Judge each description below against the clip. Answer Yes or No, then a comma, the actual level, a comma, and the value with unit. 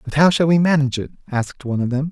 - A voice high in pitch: No, medium, 145 Hz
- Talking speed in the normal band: No, fast, 285 wpm